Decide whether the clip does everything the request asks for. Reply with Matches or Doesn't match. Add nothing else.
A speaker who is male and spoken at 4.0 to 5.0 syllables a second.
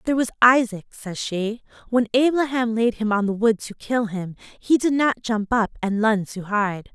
Doesn't match